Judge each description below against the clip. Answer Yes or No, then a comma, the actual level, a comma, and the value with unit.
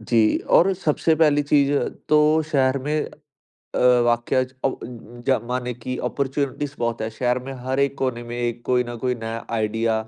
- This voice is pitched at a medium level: No, low, 130 Hz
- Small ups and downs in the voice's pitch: No, average, 3.2 semitones